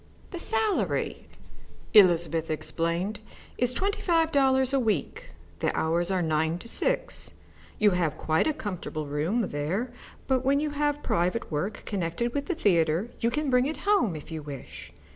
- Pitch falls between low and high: No, high, 210 Hz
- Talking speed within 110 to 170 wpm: Yes, average, 160 wpm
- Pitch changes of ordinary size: No, wide, 8.9 semitones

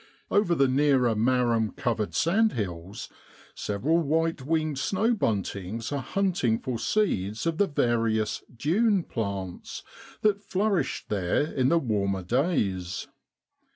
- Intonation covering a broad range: Yes, wide, 7.6 semitones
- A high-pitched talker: No, low, 130 Hz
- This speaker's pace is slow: Yes, slow, 125 wpm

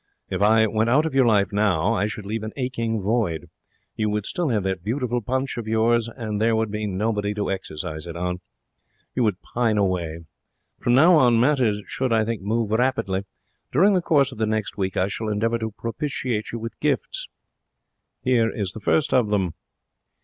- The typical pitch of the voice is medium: No, low, 110 Hz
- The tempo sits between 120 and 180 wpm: No, average, 195 wpm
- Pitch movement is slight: No, average, 3.0 semitones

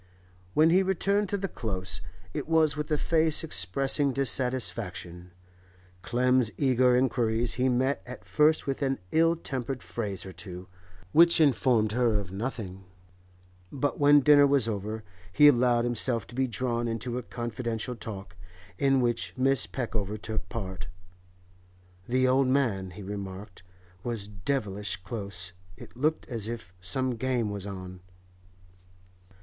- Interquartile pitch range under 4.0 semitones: No, average, 4.9 semitones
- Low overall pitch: Yes, low, 120 Hz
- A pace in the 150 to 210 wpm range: No, average, 140 wpm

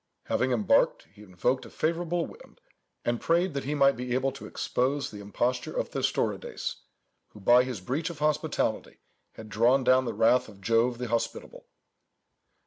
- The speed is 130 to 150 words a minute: No, average, 165 wpm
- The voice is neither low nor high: No, low, 125 Hz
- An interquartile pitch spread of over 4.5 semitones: No, average, 3.3 semitones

